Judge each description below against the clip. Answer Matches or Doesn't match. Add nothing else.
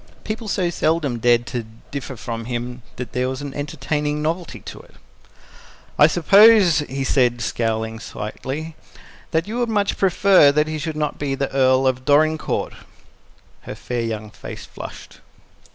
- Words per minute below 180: Matches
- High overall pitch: Doesn't match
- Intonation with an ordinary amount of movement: Matches